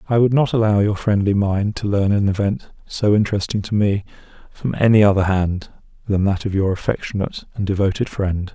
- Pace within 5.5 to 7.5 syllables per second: Yes, 5.6 syllables/s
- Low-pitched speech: Yes, low, 100 Hz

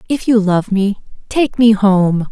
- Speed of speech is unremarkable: Yes, average, 180 wpm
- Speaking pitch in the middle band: No, high, 210 Hz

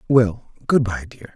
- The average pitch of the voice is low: Yes, low, 115 Hz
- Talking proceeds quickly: No, average, 175 wpm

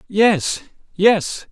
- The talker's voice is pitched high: Yes, high, 200 Hz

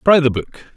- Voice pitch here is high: No, medium, 145 Hz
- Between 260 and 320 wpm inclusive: No, fast, 235 wpm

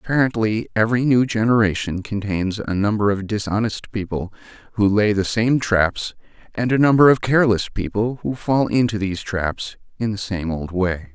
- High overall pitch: No, low, 105 Hz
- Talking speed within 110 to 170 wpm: Yes, average, 165 wpm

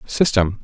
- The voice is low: Yes, low, 110 Hz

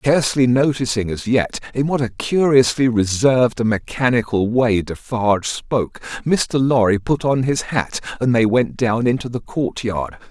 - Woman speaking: No, male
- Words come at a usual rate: Yes, average, 155 wpm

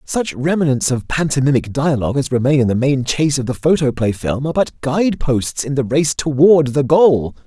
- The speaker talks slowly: No, average, 200 wpm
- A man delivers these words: Yes, male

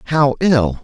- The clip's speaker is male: Yes, male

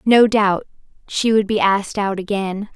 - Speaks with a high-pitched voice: Yes, high, 205 Hz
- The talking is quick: No, average, 175 wpm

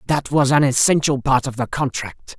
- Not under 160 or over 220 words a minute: Yes, average, 200 wpm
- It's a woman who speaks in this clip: No, male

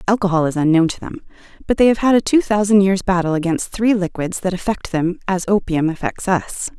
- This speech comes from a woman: Yes, female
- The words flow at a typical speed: No, fast, 210 wpm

